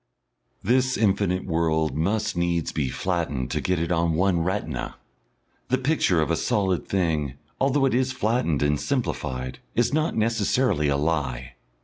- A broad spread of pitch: Yes, wide, 6.6 semitones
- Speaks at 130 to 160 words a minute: Yes, average, 150 wpm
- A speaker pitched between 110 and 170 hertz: No, very low, 90 Hz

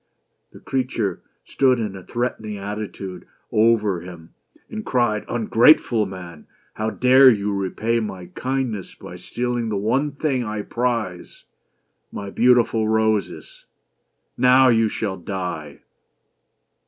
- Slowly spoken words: Yes, slow, 125 wpm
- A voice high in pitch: No, low, 110 Hz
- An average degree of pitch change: Yes, average, 3.8 semitones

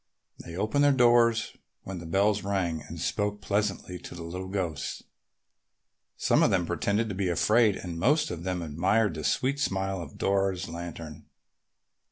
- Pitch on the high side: No, very low, 95 Hz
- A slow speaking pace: No, average, 165 wpm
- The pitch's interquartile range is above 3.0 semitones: Yes, average, 3.6 semitones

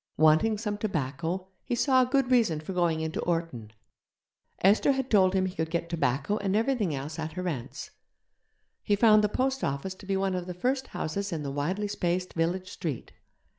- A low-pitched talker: No, medium, 185 Hz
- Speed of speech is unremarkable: Yes, average, 195 wpm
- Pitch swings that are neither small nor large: Yes, average, 4.7 semitones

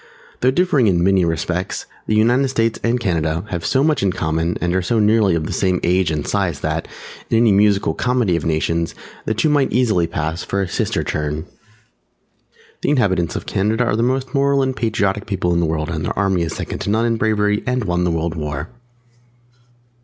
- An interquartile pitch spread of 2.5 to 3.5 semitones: No, wide, 5.5 semitones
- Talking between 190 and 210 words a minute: Yes, fast, 205 wpm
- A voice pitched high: No, very low, 95 Hz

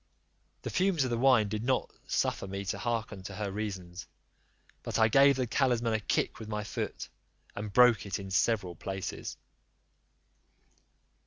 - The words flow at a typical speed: Yes, average, 160 wpm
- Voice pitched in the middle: No, low, 110 Hz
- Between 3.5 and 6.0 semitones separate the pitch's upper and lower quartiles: Yes, average, 3.8 semitones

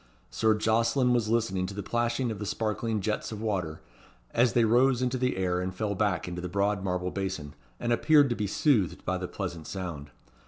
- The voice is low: Yes, low, 105 Hz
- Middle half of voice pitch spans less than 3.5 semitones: No, average, 4.3 semitones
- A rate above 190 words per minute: Yes, fast, 205 wpm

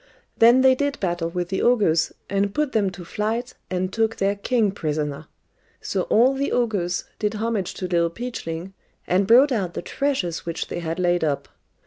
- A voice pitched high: Yes, high, 195 Hz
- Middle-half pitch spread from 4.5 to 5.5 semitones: Yes, average, 5.1 semitones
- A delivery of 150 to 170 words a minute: No, average, 180 wpm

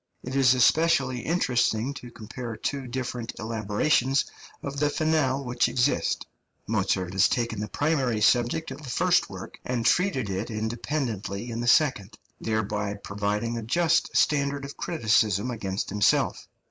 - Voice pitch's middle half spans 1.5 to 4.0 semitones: No, average, 4.4 semitones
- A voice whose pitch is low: Yes, low, 120 Hz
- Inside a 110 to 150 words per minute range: Yes, average, 145 wpm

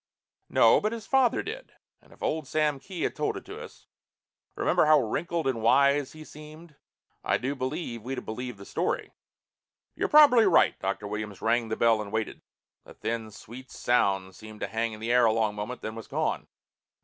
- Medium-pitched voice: No, low, 125 Hz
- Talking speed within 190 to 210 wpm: Yes, average, 195 wpm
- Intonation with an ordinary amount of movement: No, wide, 6.0 semitones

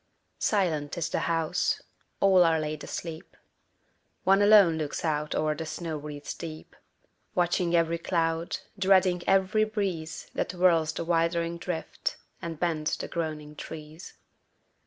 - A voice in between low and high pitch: Yes, medium, 165 Hz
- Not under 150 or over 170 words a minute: No, slow, 135 wpm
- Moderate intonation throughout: No, narrow, 2.3 semitones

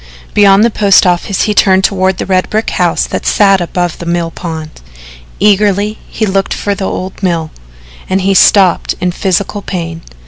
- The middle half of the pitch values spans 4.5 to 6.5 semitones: No, narrow, 2.4 semitones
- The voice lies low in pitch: No, high, 190 Hz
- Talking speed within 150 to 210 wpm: Yes, average, 175 wpm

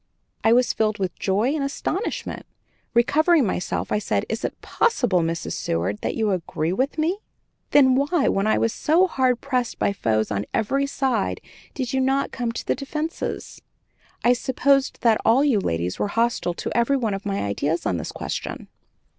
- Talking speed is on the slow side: No, average, 180 wpm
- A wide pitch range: Yes, wide, 6.0 semitones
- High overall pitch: Yes, high, 235 Hz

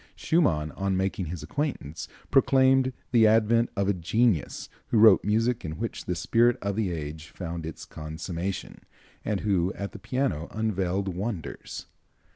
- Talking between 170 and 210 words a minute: No, average, 150 wpm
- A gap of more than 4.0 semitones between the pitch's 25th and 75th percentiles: Yes, average, 5.1 semitones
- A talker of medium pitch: No, low, 100 Hz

